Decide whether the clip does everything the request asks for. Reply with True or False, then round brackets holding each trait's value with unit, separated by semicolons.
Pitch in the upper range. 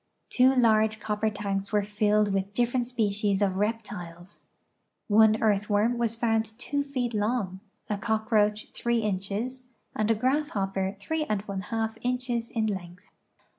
True (215 Hz)